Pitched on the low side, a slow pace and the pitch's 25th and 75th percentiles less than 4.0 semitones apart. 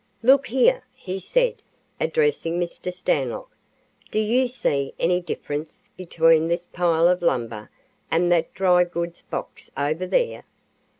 No: medium, 175 Hz; slow, 130 wpm; average, 2.9 semitones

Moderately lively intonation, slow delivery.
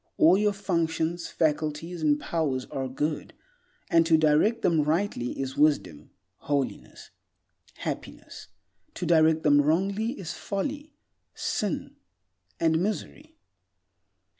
Yes: average, 4.5 semitones; slow, 110 wpm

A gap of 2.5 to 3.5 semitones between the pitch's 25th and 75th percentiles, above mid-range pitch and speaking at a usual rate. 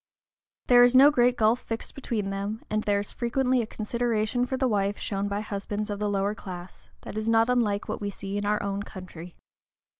No: average, 3.0 semitones; high, 210 Hz; fast, 210 wpm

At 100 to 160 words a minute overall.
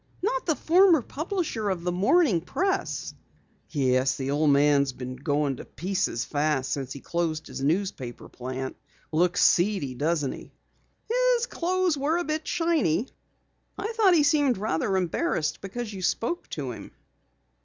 Yes: average, 150 wpm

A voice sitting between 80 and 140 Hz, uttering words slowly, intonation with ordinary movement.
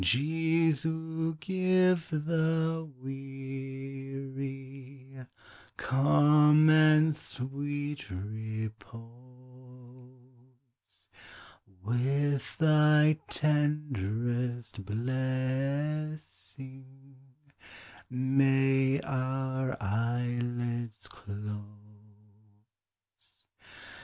Yes: low, 135 Hz; slow, 40 wpm; average, 3.4 semitones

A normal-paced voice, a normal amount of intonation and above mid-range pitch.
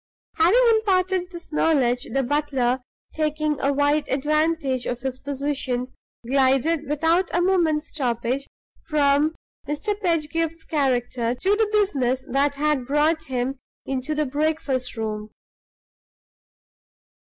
No: slow, 115 wpm; average, 3.7 semitones; very high, 290 Hz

